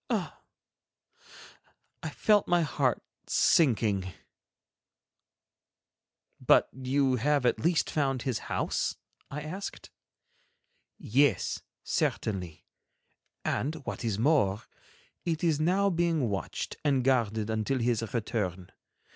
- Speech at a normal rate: No, slow, 100 wpm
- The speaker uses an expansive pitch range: Yes, wide, 5.8 semitones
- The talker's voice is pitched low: Yes, low, 130 Hz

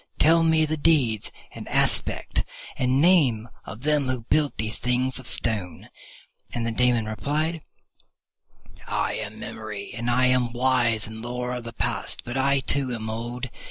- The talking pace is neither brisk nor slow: Yes, average, 160 wpm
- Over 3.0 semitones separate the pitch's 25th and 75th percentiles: Yes, average, 3.4 semitones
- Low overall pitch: Yes, low, 125 Hz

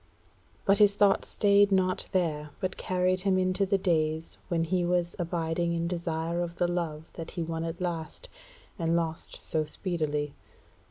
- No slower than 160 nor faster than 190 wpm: Yes, average, 165 wpm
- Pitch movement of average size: No, narrow, 2.2 semitones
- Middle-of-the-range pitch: Yes, medium, 175 Hz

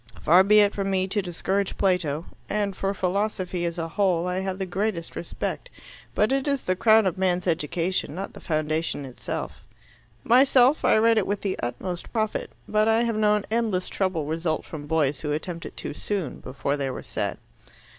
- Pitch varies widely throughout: No, average, 4.1 semitones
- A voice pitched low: No, medium, 185 Hz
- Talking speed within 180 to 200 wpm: Yes, average, 190 wpm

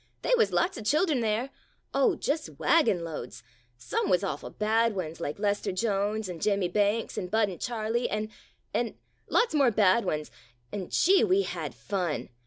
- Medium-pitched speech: No, high, 215 Hz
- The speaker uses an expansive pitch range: No, average, 4.7 semitones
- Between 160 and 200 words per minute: Yes, average, 195 wpm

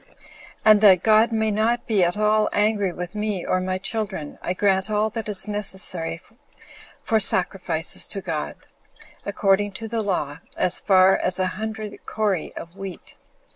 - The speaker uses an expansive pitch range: No, narrow, 2.6 semitones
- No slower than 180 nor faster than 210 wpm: No, average, 165 wpm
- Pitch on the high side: Yes, high, 200 Hz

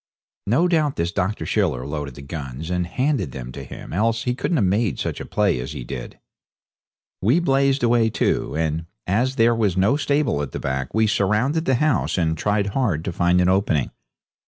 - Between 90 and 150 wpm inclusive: No, average, 195 wpm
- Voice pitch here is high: No, low, 100 Hz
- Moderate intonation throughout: No, wide, 7.4 semitones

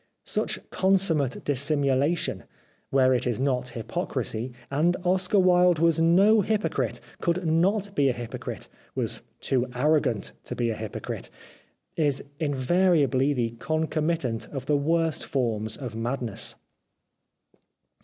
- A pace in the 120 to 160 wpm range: Yes, slow, 135 wpm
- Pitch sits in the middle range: Yes, medium, 145 Hz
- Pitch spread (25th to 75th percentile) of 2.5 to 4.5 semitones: No, average, 5.3 semitones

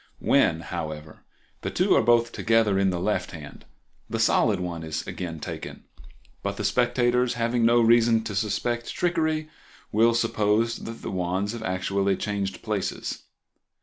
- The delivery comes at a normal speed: Yes, average, 150 wpm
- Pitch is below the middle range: Yes, low, 105 Hz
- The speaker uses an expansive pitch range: No, average, 3.8 semitones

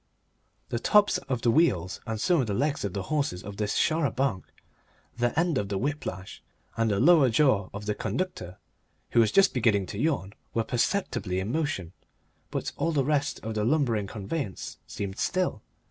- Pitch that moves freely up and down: Yes, wide, 6.7 semitones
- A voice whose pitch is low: Yes, low, 115 Hz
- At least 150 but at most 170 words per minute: No, average, 190 wpm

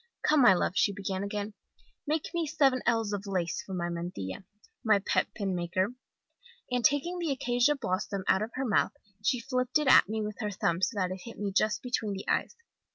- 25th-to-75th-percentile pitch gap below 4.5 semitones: No, average, 4.9 semitones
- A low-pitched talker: No, high, 210 Hz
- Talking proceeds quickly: Yes, fast, 210 wpm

